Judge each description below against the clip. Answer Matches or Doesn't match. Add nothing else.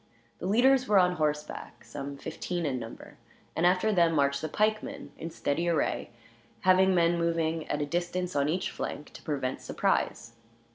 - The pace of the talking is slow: Doesn't match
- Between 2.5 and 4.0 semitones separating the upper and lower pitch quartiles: Matches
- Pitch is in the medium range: Matches